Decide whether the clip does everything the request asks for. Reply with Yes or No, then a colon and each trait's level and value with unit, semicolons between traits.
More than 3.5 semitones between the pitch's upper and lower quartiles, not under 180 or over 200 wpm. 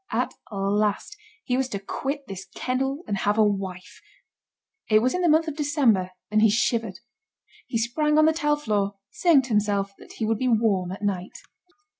Yes: wide, 5.6 semitones; average, 190 wpm